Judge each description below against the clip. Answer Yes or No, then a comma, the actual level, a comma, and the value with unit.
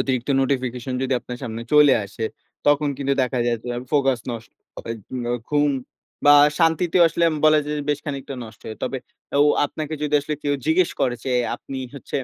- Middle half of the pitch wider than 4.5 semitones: No, average, 3.2 semitones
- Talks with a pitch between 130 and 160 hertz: Yes, medium, 140 Hz